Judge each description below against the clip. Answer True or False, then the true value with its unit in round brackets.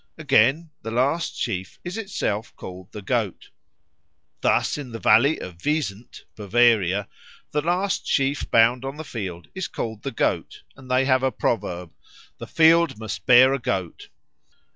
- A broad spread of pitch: True (5.9 semitones)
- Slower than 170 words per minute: True (160 wpm)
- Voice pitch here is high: False (120 Hz)